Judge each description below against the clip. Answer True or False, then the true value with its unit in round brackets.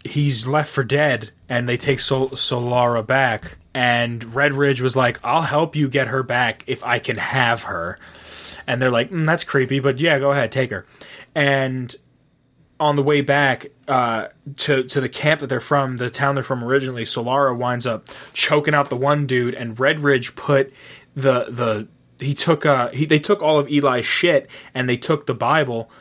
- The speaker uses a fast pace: False (190 wpm)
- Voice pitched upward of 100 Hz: True (135 Hz)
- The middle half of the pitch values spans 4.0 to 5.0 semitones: False (2.7 semitones)